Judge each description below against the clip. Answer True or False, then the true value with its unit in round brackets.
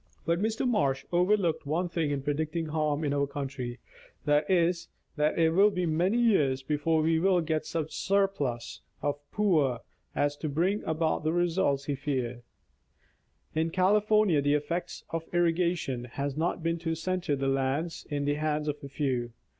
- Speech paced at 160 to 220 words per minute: True (170 wpm)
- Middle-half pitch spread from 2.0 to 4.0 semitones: True (3.5 semitones)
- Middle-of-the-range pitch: True (155 Hz)